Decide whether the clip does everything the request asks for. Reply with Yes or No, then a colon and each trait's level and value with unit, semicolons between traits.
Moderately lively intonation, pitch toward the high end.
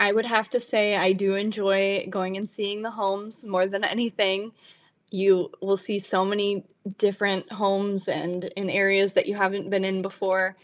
No: narrow, 1.3 semitones; high, 195 Hz